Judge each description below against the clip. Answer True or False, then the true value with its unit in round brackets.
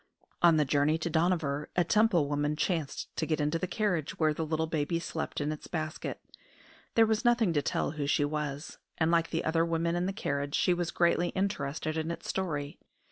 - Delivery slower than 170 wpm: False (205 wpm)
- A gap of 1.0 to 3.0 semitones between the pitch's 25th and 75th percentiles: True (2.7 semitones)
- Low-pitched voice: False (160 Hz)